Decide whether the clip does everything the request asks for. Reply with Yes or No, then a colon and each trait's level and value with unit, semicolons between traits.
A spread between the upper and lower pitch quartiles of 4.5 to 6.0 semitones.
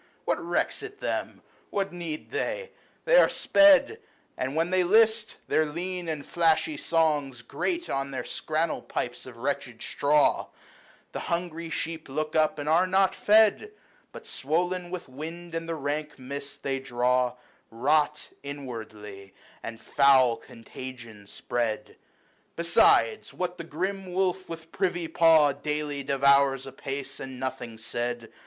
Yes: average, 4.9 semitones